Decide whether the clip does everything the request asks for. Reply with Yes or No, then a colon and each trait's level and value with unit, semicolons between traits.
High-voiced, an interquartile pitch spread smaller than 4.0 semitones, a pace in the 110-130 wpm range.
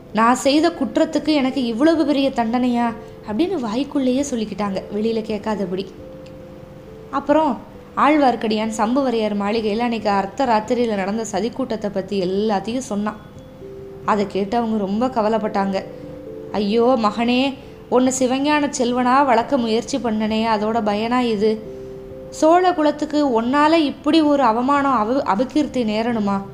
No: high, 235 Hz; average, 4.3 semitones; average, 115 wpm